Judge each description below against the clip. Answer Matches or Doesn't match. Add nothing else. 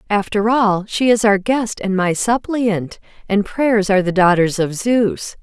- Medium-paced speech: Matches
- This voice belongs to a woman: Matches